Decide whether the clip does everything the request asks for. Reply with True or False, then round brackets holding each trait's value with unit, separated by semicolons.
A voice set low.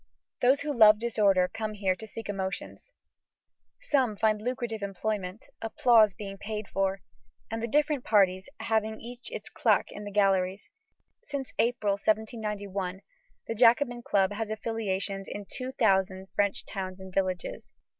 False (210 Hz)